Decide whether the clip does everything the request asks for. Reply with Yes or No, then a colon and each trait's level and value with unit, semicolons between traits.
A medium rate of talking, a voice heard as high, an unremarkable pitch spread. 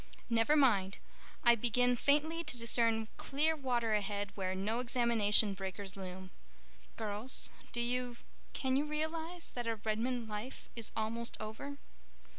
No: slow, 125 wpm; high, 235 Hz; average, 3.6 semitones